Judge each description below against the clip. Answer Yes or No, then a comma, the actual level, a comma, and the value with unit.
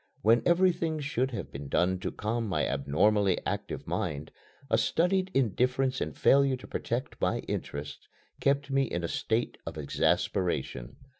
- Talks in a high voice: No, low, 115 Hz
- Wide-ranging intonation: Yes, wide, 8.2 semitones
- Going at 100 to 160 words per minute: Yes, average, 150 wpm